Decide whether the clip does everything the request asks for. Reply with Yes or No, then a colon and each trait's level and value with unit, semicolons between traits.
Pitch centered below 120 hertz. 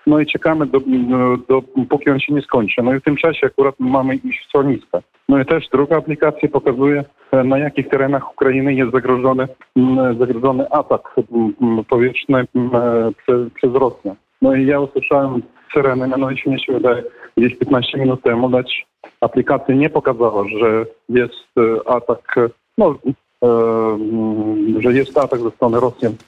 No: low, 130 Hz